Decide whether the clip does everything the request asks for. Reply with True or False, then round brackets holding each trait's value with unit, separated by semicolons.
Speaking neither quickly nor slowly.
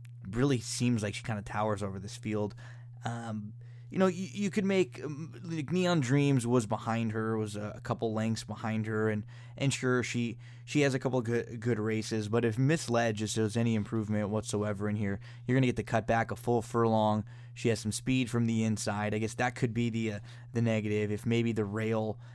False (220 wpm)